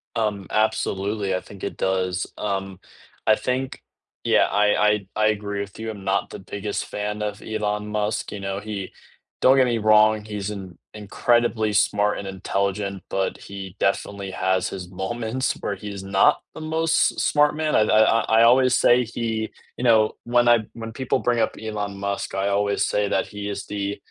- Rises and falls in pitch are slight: Yes, narrow, 2.1 semitones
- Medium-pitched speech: No, low, 105 Hz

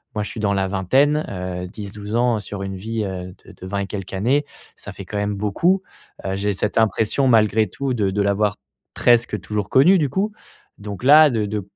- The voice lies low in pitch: Yes, low, 105 Hz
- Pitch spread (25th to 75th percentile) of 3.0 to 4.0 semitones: Yes, average, 3.6 semitones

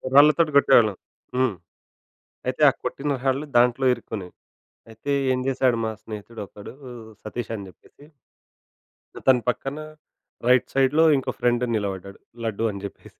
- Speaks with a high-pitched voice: No, low, 125 Hz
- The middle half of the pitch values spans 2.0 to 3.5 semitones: No, average, 3.9 semitones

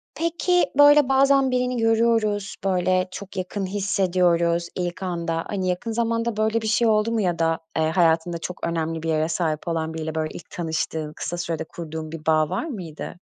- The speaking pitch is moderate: Yes, medium, 180 Hz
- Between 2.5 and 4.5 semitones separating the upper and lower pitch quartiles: No, wide, 5.4 semitones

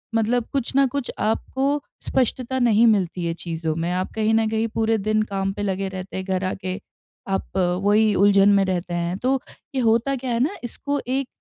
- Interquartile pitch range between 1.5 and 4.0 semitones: No, average, 4.5 semitones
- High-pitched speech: Yes, high, 215 Hz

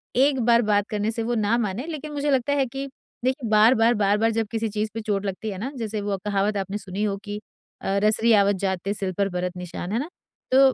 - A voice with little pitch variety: No, average, 3.0 semitones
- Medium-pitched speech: No, high, 215 Hz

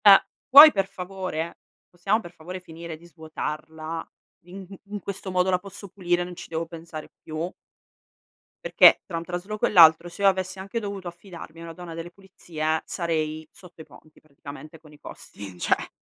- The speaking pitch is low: No, medium, 175 Hz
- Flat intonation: No, average, 3.0 semitones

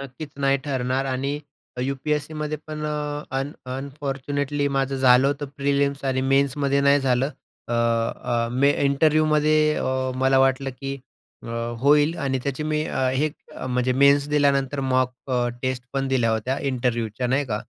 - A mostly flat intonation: Yes, narrow, 1.8 semitones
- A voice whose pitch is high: No, low, 135 Hz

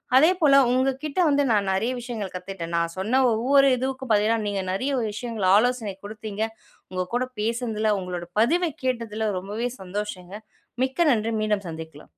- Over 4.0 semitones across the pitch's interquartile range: Yes, average, 4.5 semitones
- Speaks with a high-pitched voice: Yes, high, 220 Hz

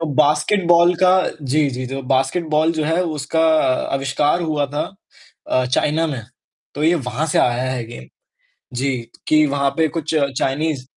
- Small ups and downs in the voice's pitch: No, average, 3.3 semitones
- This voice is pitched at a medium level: Yes, medium, 150 Hz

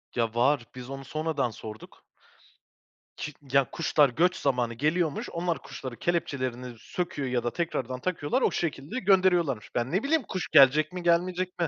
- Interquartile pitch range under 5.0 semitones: No, wide, 5.4 semitones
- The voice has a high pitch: No, medium, 145 Hz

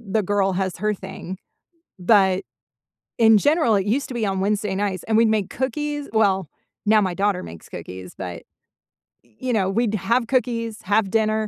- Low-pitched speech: No, high, 210 Hz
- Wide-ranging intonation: No, average, 3.2 semitones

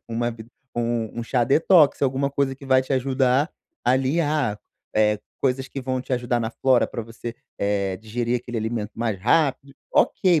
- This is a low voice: Yes, low, 125 Hz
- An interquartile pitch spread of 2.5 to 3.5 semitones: Yes, average, 2.9 semitones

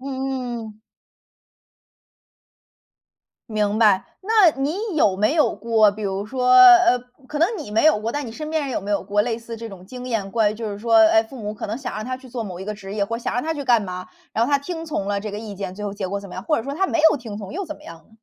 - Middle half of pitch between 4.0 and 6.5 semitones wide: Yes, average, 4.7 semitones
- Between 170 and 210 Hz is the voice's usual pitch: No, high, 225 Hz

